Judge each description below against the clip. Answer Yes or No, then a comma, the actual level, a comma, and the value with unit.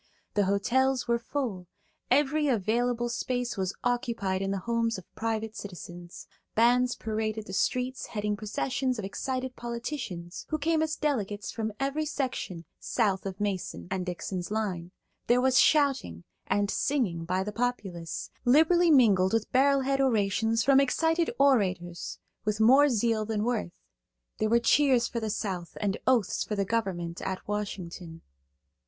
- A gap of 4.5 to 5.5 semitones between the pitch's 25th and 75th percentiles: Yes, average, 4.9 semitones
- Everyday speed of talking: Yes, average, 150 wpm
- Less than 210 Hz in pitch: No, high, 225 Hz